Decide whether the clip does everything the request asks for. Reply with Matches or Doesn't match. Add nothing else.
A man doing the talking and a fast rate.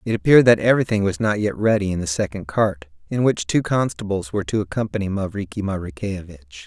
Doesn't match